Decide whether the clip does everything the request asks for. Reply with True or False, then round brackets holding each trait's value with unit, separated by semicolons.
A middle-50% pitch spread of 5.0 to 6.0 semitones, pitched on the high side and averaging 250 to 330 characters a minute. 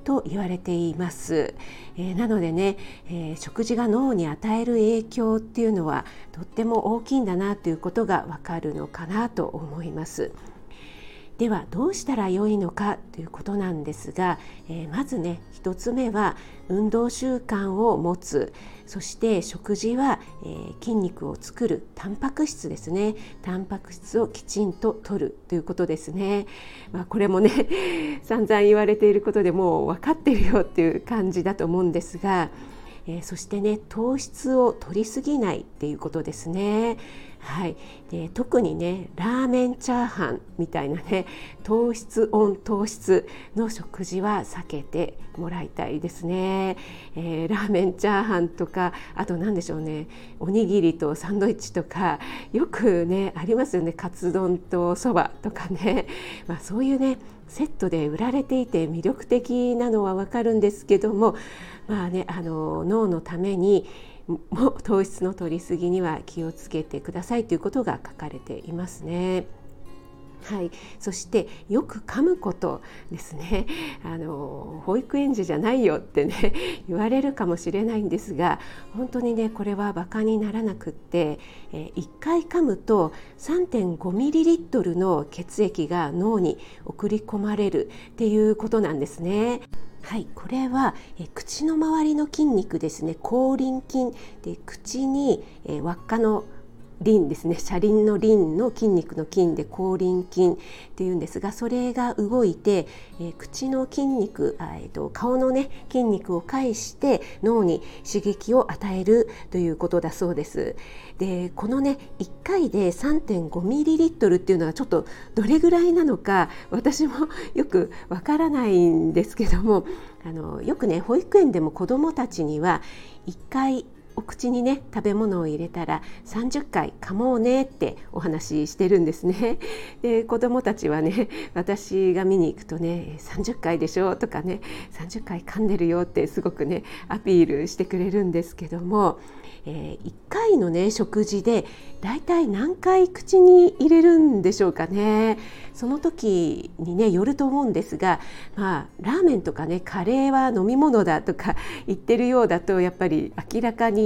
True (5.3 semitones; 200 Hz; 310 characters per minute)